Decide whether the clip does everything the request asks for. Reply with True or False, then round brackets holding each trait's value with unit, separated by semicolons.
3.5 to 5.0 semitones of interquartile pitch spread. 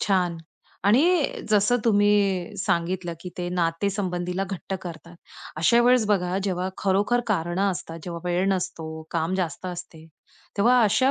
False (2.8 semitones)